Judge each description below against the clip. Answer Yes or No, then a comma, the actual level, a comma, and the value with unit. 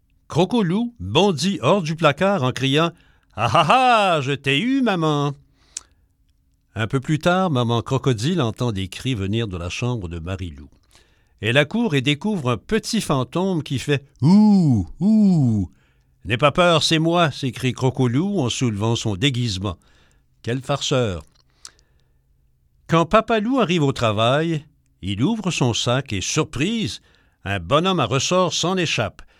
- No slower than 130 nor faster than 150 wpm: Yes, slow, 145 wpm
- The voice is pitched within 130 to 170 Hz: Yes, low, 135 Hz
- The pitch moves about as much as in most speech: No, wide, 8.5 semitones